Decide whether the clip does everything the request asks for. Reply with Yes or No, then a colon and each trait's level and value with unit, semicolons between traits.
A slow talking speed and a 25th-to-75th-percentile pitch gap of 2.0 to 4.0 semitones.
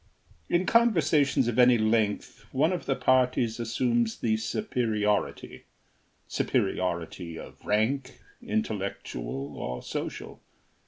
No: slow, 100 wpm; average, 4.6 semitones